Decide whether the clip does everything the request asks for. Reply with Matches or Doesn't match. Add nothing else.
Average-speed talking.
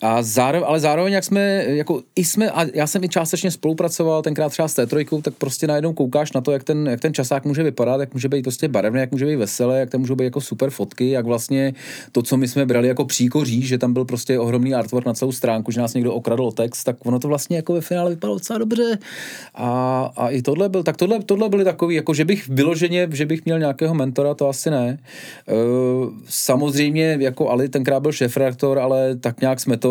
Doesn't match